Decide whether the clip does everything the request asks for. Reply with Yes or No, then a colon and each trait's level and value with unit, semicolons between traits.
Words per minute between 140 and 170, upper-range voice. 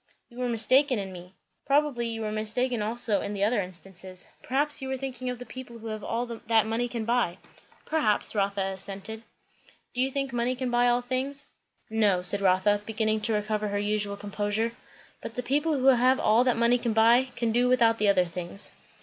No: average, 200 wpm; high, 225 Hz